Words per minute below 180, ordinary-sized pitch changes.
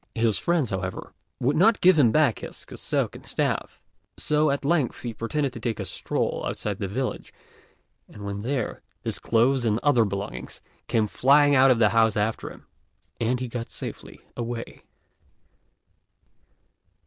Yes: average, 160 wpm; average, 4.3 semitones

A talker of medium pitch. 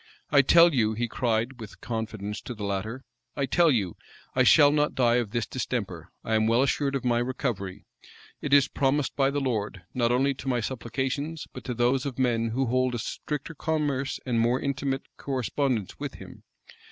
No: low, 125 Hz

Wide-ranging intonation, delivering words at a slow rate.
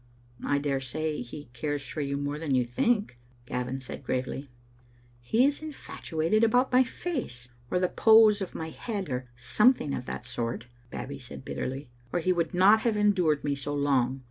No: wide, 8.0 semitones; average, 185 wpm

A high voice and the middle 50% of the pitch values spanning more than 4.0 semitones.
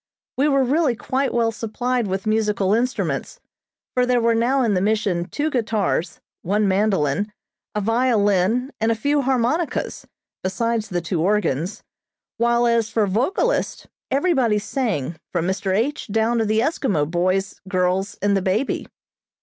Yes: high, 220 Hz; average, 4.4 semitones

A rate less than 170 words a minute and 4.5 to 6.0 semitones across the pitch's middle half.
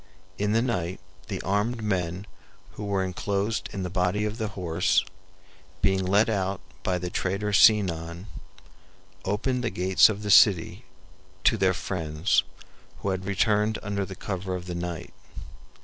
No: average, 150 wpm; narrow, 2.5 semitones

